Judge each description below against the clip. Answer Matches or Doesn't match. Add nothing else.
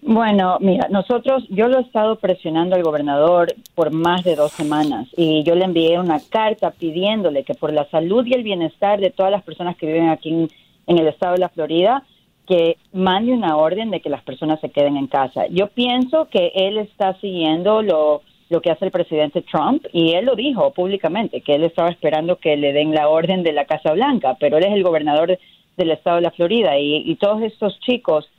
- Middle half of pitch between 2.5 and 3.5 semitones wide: Doesn't match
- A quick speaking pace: Matches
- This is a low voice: Doesn't match